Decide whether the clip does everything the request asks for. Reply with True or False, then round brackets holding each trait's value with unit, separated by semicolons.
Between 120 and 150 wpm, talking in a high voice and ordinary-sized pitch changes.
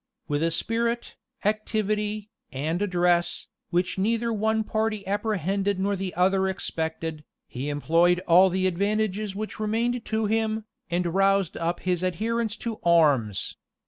True (140 wpm; 195 Hz; 3.8 semitones)